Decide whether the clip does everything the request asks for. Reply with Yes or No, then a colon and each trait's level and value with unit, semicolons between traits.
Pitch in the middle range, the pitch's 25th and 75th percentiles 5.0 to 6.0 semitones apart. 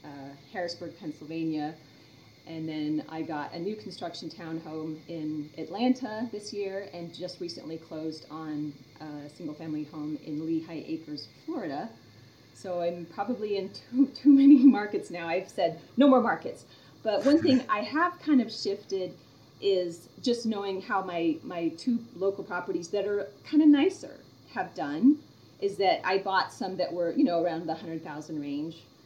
Yes: medium, 170 Hz; wide, 5.5 semitones